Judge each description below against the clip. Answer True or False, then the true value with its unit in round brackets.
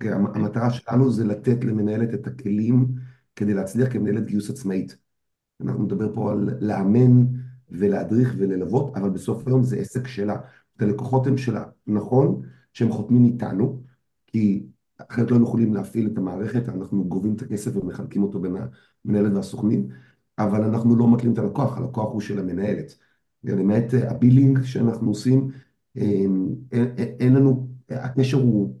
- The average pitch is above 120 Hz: False (110 Hz)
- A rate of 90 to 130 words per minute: False (145 wpm)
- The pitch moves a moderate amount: True (3.6 semitones)